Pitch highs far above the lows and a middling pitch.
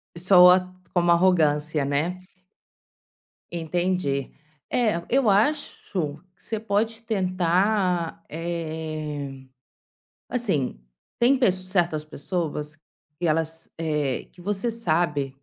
No: average, 4.0 semitones; medium, 175 Hz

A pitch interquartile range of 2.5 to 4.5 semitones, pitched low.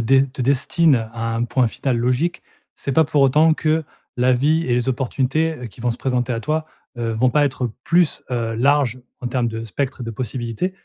Yes: average, 3.5 semitones; low, 130 Hz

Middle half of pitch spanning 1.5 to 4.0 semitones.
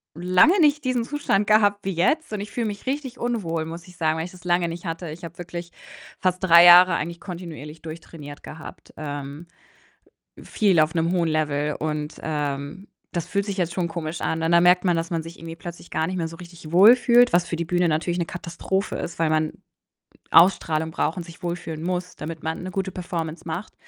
Yes: narrow, 2.4 semitones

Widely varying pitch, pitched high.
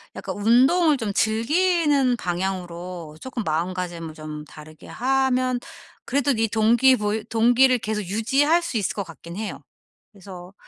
Yes: wide, 6.3 semitones; high, 220 Hz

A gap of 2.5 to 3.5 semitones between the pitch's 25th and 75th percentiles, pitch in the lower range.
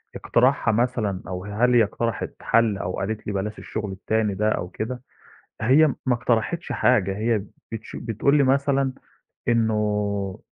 Yes: average, 3.2 semitones; low, 110 Hz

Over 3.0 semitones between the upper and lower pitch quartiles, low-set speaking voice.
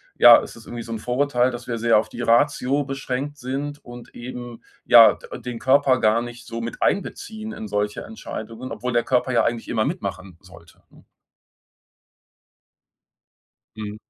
No: average, 2.7 semitones; low, 120 Hz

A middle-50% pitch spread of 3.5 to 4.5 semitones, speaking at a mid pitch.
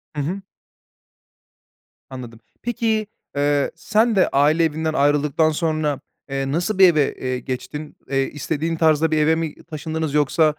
No: narrow, 2.4 semitones; medium, 155 Hz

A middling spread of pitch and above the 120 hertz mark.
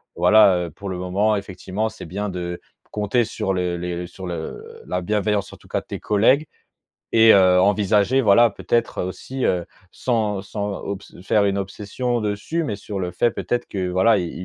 No: average, 3.0 semitones; low, 100 Hz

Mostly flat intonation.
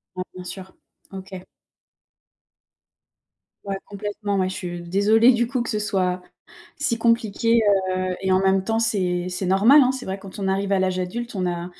No: average, 3.3 semitones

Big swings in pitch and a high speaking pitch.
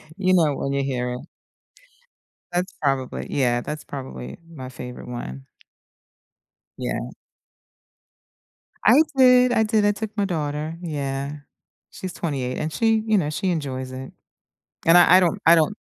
No: wide, 6.1 semitones; medium, 155 Hz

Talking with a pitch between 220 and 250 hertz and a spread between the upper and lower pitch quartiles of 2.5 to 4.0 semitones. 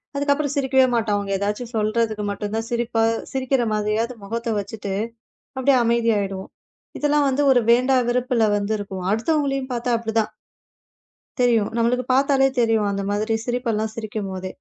Yes: high, 230 Hz; average, 3.5 semitones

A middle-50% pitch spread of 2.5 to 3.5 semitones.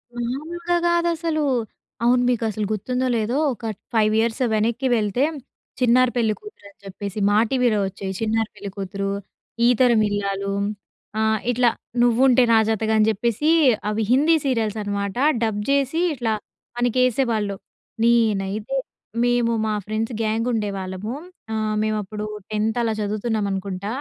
Yes: average, 3.0 semitones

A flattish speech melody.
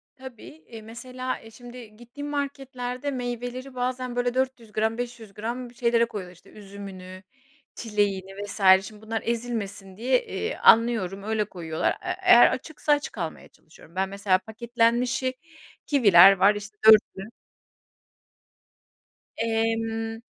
No: average, 3.5 semitones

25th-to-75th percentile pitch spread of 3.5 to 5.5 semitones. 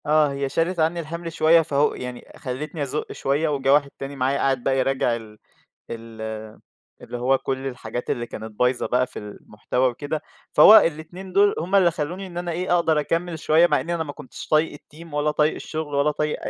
Yes: average, 3.8 semitones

